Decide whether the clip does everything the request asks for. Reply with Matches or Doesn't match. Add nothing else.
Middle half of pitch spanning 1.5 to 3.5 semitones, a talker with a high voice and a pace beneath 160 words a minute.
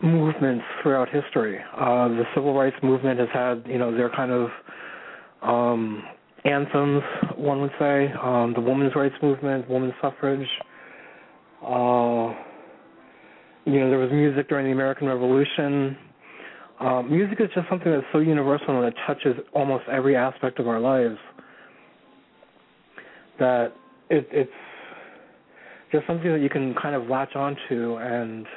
Doesn't match